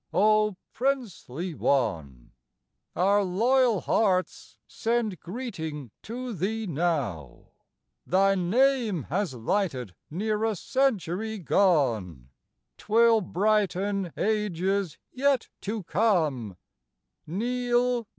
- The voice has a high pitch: Yes, high, 195 Hz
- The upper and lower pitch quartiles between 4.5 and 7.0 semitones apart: Yes, wide, 5.5 semitones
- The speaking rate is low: Yes, slow, 90 wpm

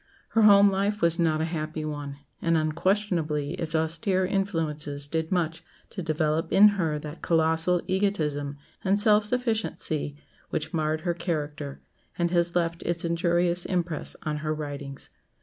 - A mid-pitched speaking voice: Yes, medium, 165 Hz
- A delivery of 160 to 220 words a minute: No, average, 150 wpm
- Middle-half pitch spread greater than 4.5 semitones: No, average, 3.1 semitones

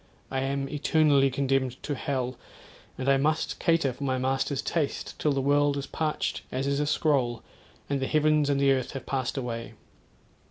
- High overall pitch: No, medium, 140 Hz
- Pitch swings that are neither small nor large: No, narrow, 1.7 semitones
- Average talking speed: Yes, average, 185 wpm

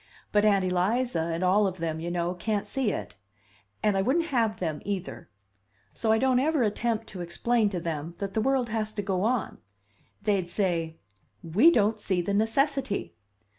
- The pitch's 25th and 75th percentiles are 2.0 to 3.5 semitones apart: No, average, 4.4 semitones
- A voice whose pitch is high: Yes, high, 205 Hz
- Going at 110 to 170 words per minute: No, average, 180 wpm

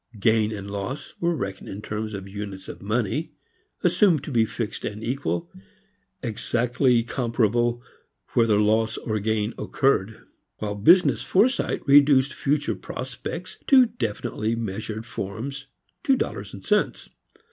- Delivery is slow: Yes, slow, 130 wpm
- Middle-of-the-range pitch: No, low, 115 Hz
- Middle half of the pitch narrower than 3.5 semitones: No, average, 4.5 semitones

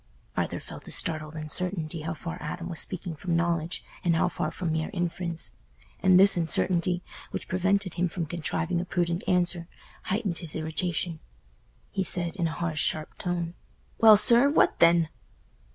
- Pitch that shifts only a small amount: Yes, narrow, 1.9 semitones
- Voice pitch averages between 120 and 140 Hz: No, medium, 170 Hz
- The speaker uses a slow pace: No, average, 165 wpm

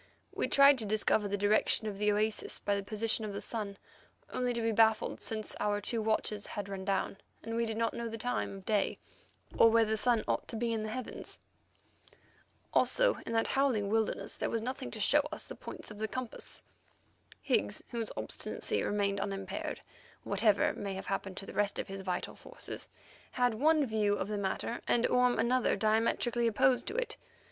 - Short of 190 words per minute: No, average, 195 wpm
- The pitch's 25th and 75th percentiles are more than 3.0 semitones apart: No, narrow, 2.5 semitones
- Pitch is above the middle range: Yes, high, 220 Hz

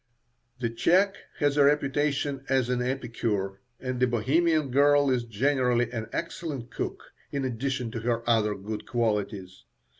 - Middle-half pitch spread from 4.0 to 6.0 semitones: No, average, 3.6 semitones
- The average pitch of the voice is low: Yes, low, 125 Hz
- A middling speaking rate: Yes, average, 145 wpm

